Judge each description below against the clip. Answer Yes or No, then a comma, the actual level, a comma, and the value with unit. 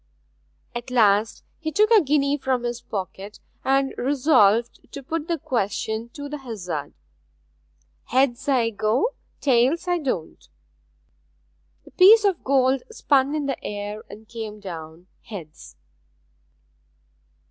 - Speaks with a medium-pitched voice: No, very high, 250 Hz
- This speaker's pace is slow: Yes, slow, 125 wpm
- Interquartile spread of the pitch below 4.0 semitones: No, average, 5.3 semitones